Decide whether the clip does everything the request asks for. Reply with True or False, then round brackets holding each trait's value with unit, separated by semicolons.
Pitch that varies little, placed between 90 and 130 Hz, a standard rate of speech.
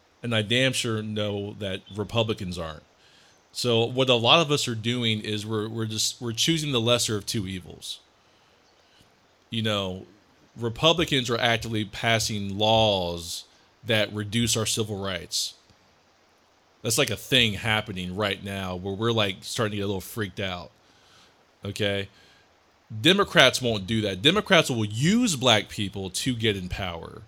False (3.1 semitones; 110 Hz; 155 wpm)